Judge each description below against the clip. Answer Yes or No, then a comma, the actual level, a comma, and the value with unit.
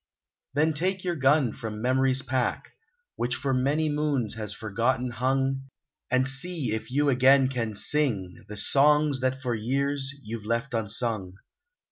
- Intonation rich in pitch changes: No, average, 3.4 semitones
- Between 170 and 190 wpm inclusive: No, average, 145 wpm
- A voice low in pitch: Yes, low, 130 Hz